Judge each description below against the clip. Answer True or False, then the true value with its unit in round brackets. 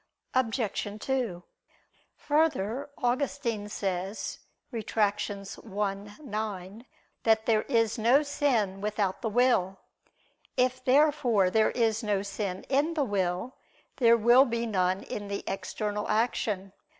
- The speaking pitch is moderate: False (220 Hz)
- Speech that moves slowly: True (115 wpm)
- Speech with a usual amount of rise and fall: True (3.9 semitones)